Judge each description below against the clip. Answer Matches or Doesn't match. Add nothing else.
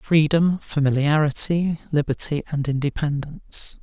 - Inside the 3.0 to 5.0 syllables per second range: Matches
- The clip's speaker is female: Doesn't match